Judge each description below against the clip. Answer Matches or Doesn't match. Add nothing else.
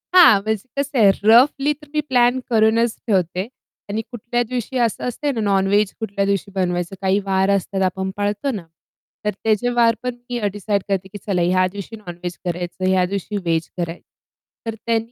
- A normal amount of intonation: Matches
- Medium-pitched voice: Doesn't match